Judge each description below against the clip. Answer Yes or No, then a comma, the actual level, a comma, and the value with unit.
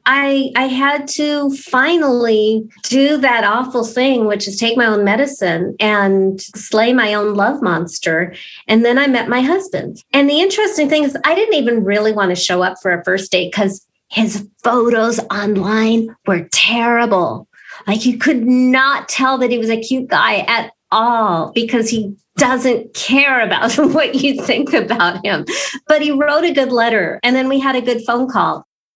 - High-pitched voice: Yes, high, 235 Hz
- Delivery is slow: No, average, 180 wpm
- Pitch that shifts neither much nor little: Yes, average, 4.6 semitones